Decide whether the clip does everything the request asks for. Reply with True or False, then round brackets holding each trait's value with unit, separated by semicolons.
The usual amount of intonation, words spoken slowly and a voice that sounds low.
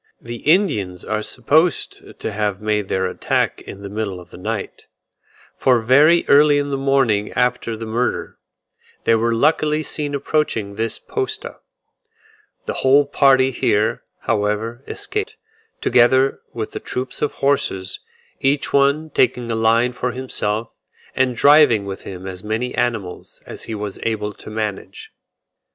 False (4.7 semitones; 145 wpm; 120 Hz)